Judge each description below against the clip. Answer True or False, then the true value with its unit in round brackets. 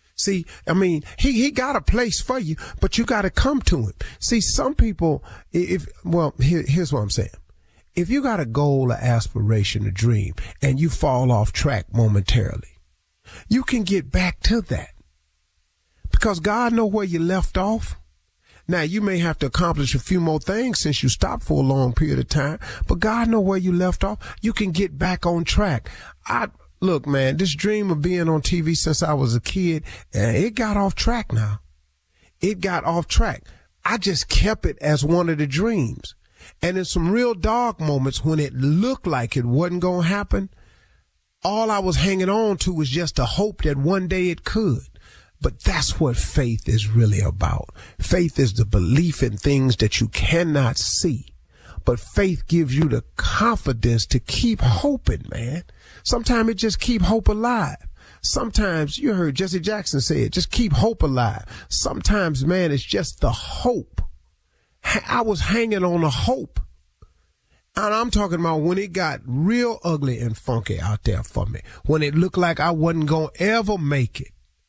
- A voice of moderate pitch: True (155 Hz)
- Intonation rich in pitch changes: True (8.8 semitones)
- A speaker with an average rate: True (185 wpm)